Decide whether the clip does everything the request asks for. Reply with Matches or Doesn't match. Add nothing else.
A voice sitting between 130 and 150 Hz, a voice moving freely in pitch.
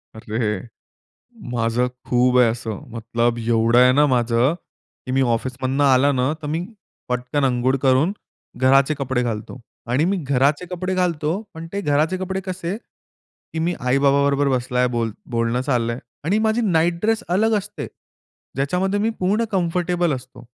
Matches